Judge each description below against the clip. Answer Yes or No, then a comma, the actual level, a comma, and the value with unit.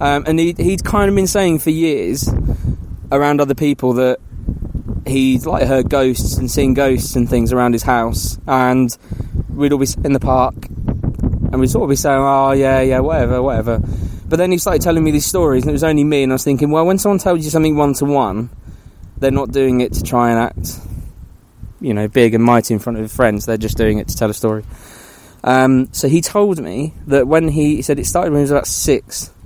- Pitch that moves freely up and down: No, average, 3.9 semitones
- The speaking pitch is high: No, low, 135 Hz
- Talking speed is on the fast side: Yes, fast, 225 wpm